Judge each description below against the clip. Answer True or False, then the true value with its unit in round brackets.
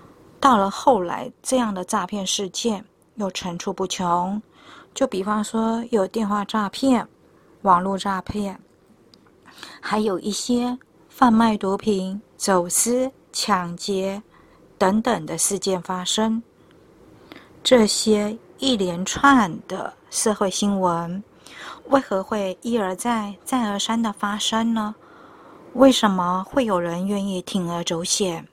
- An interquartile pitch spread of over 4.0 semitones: False (3.2 semitones)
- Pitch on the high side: True (205 Hz)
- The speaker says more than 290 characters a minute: False (175 characters per minute)